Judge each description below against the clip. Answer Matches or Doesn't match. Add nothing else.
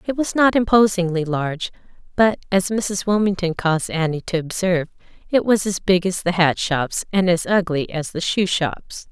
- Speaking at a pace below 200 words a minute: Matches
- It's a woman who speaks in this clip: Matches